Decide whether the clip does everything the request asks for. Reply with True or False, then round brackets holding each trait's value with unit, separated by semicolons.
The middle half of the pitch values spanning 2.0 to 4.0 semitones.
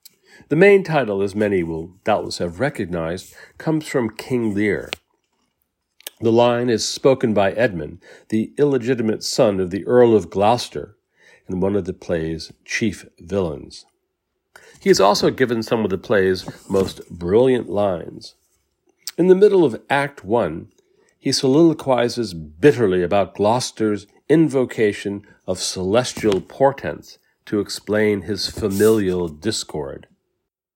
False (5.3 semitones)